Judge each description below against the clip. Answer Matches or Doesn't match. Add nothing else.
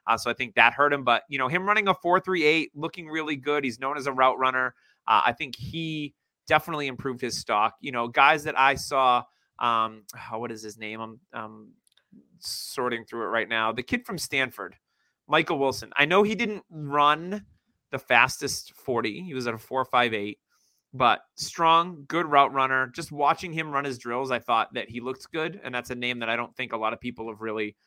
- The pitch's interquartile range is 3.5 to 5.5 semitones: Matches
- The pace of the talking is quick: Matches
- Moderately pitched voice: Doesn't match